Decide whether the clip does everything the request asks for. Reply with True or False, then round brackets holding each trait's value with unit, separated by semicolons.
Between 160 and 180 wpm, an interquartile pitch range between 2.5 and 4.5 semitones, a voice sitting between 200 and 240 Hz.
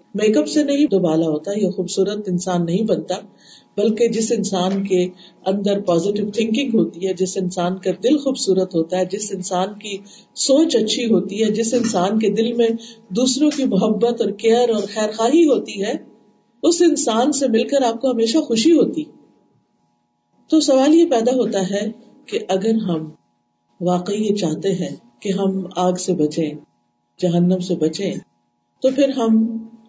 True (170 wpm; 4.2 semitones; 205 Hz)